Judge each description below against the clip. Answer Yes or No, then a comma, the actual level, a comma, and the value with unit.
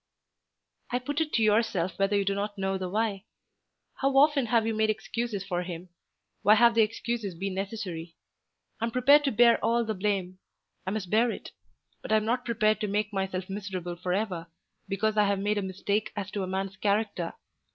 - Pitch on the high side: Yes, high, 205 Hz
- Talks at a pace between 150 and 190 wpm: No, fast, 205 wpm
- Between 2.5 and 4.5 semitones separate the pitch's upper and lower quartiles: Yes, average, 2.9 semitones